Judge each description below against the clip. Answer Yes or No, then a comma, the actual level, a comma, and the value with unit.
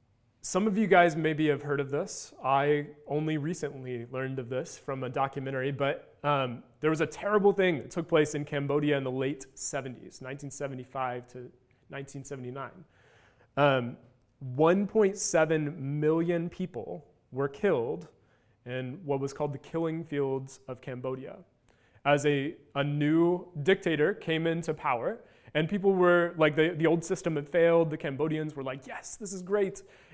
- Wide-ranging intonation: No, average, 3.7 semitones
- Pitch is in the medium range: Yes, medium, 145 Hz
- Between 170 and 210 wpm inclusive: No, average, 155 wpm